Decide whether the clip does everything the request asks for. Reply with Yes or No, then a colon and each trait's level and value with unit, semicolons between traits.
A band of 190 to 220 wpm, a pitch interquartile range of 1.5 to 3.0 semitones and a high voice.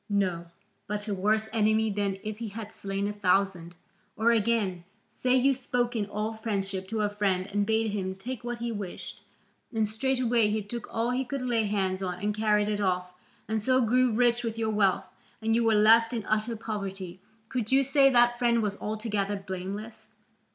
Yes: average, 195 wpm; average, 2.7 semitones; high, 215 Hz